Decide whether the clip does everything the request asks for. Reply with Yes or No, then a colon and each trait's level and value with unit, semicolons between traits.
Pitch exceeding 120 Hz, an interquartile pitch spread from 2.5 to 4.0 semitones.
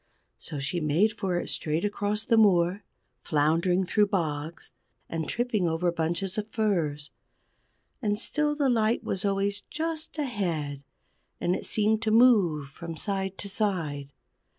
No: high, 190 Hz; average, 4.8 semitones